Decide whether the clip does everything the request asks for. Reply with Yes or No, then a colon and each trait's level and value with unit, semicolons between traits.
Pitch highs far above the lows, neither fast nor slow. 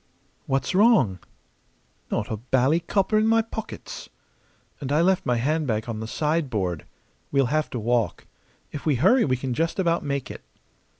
Yes: wide, 5.9 semitones; average, 165 wpm